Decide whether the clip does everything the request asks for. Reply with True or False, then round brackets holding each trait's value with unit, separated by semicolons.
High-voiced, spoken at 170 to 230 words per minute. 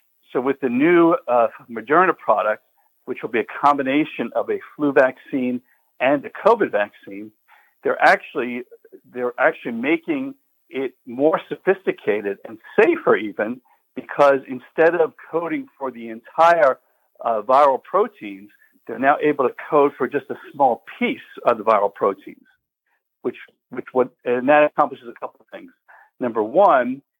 False (195 Hz; 150 wpm)